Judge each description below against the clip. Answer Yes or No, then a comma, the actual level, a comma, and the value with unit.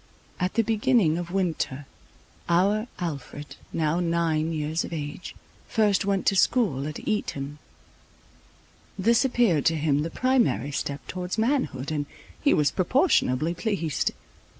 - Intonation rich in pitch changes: Yes, wide, 5.8 semitones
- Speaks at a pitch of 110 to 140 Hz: No, medium, 170 Hz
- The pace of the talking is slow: Yes, slow, 130 wpm